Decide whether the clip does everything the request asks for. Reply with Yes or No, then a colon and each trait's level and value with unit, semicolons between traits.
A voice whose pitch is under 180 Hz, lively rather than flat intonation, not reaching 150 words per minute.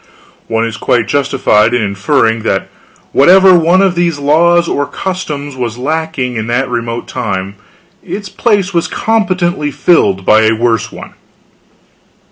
Yes: medium, 140 Hz; wide, 7.1 semitones; average, 140 wpm